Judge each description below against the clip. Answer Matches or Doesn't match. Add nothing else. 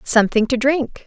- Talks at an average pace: Matches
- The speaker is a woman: Matches